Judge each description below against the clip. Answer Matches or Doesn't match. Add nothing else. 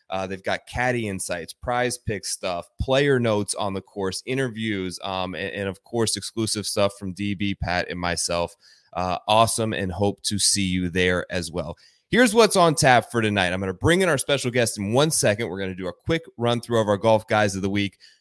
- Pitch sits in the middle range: Doesn't match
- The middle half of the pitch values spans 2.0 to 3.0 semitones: Doesn't match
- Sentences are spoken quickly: Matches